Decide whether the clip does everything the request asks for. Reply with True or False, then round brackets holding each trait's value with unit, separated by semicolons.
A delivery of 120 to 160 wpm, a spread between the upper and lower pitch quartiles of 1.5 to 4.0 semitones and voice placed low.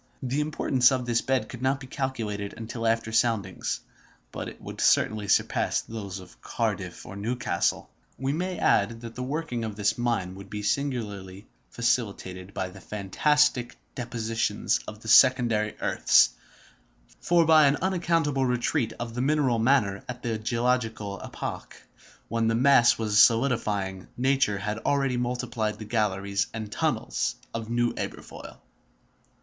True (145 wpm; 3.7 semitones; 115 Hz)